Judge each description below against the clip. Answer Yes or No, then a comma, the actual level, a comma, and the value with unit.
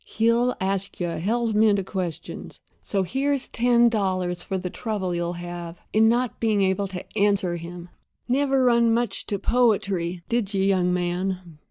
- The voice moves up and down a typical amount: Yes, average, 4.5 semitones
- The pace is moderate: Yes, average, 170 wpm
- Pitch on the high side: Yes, high, 195 Hz